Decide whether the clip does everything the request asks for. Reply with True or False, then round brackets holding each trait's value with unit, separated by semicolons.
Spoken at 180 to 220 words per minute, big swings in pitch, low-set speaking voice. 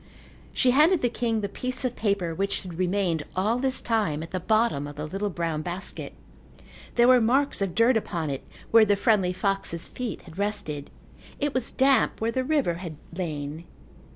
False (185 wpm; 5.9 semitones; 200 Hz)